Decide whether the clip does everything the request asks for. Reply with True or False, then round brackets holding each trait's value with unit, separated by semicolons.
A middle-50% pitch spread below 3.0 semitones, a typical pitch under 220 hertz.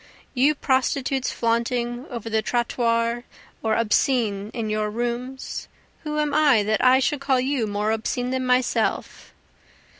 False (2.6 semitones; 240 Hz)